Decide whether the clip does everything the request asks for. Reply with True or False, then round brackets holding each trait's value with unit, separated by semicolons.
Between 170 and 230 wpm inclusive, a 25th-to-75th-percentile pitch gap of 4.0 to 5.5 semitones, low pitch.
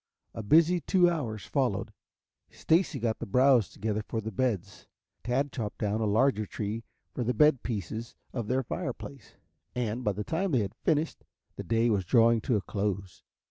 True (180 wpm; 4.3 semitones; 115 Hz)